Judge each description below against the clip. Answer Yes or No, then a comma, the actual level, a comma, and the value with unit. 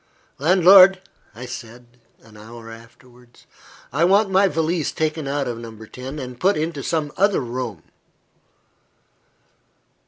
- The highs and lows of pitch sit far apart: Yes, wide, 6.2 semitones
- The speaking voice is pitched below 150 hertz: Yes, medium, 140 Hz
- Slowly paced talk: Yes, slow, 125 wpm